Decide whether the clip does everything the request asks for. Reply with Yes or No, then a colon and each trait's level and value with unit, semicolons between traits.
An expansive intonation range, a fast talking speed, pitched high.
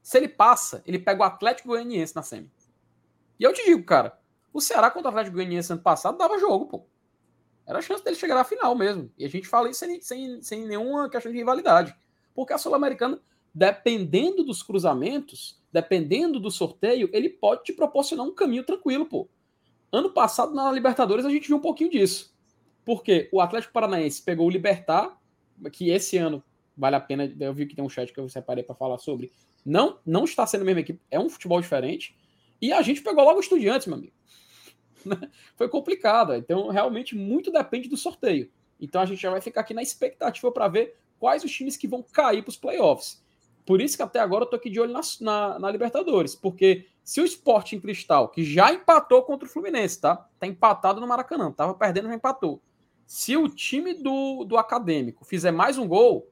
Yes: wide, 8.2 semitones; fast, 205 wpm; high, 235 Hz